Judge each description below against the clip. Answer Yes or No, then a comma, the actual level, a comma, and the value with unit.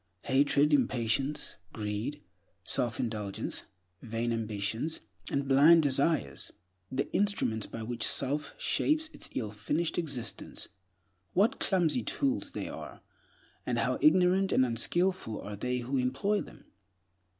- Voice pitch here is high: No, low, 135 Hz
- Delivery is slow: Yes, slow, 115 wpm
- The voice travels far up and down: Yes, wide, 6.4 semitones